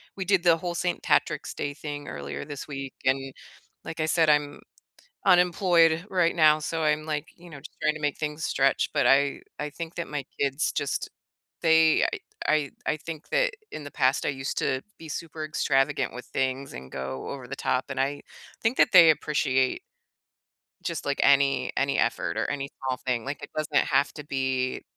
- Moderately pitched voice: Yes, medium, 145 Hz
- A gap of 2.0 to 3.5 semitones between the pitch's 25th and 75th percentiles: Yes, average, 3.0 semitones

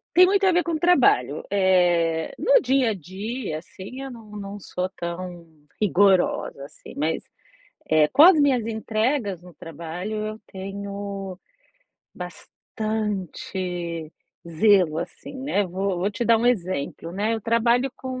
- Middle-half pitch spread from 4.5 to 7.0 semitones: Yes, average, 4.8 semitones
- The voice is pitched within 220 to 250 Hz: No, high, 200 Hz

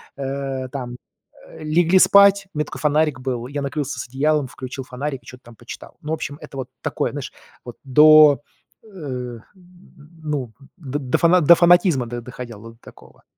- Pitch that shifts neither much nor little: Yes, average, 3.4 semitones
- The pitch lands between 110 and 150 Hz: Yes, medium, 140 Hz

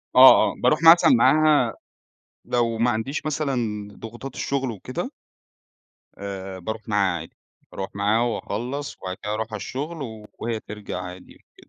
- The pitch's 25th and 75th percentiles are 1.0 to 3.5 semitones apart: No, average, 4.9 semitones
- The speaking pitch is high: No, low, 115 Hz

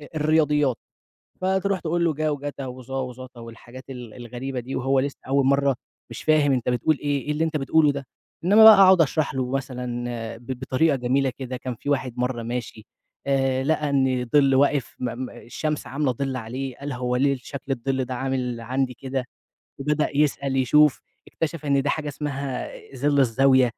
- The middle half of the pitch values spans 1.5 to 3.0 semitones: Yes, narrow, 2.5 semitones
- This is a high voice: No, low, 135 Hz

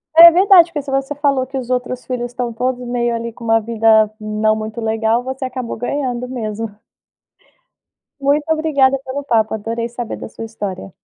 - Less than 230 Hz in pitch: No, high, 245 Hz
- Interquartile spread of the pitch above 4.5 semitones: No, average, 3.2 semitones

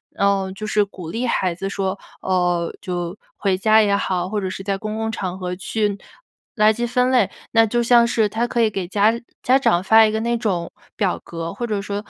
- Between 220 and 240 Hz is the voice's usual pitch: No, high, 205 Hz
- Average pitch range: Yes, average, 3.1 semitones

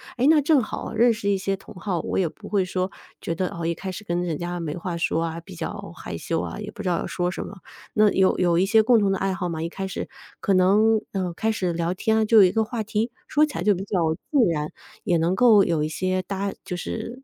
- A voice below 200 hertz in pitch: Yes, high, 190 Hz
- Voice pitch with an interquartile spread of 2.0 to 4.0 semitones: Yes, average, 3.7 semitones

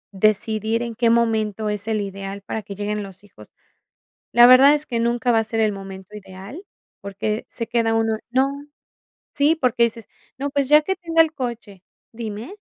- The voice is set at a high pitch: Yes, high, 225 Hz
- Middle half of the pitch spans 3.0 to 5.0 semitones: Yes, average, 3.4 semitones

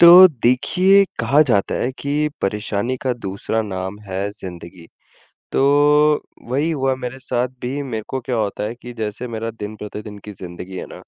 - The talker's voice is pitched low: Yes, low, 115 Hz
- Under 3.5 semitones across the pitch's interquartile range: No, average, 4.5 semitones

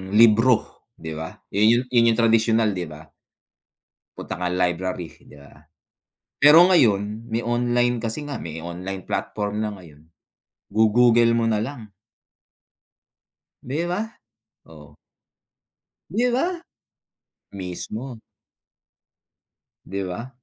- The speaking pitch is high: No, low, 110 Hz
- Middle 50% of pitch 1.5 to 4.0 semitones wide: No, average, 4.8 semitones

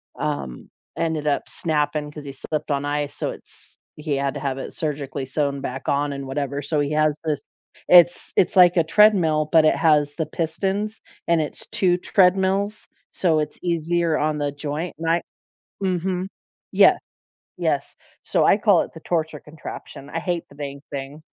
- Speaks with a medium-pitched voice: Yes, medium, 155 Hz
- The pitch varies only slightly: No, average, 3.1 semitones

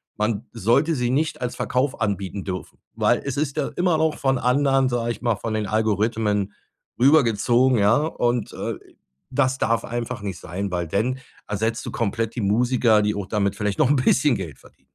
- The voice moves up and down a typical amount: Yes, average, 4.1 semitones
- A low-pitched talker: Yes, low, 115 Hz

